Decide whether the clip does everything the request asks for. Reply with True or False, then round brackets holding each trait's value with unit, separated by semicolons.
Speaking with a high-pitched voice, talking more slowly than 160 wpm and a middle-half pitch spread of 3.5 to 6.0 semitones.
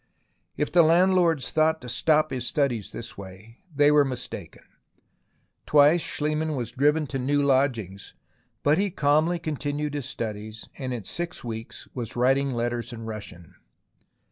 False (140 Hz; 150 wpm; 4.6 semitones)